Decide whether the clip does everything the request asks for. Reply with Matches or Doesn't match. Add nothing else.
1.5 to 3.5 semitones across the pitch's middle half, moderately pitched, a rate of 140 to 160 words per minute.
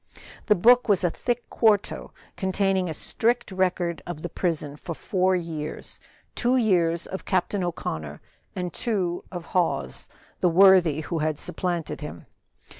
Matches